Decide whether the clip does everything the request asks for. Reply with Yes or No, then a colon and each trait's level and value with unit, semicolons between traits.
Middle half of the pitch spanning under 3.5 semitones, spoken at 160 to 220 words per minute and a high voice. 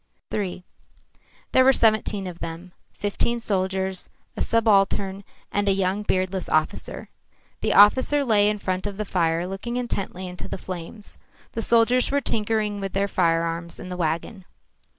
No: average, 2.9 semitones; average, 150 wpm; high, 195 Hz